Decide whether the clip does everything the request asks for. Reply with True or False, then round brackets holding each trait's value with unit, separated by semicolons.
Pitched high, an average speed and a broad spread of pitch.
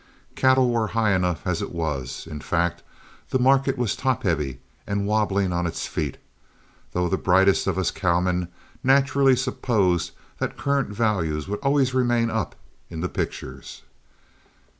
False (100 Hz; 150 wpm; 6.2 semitones)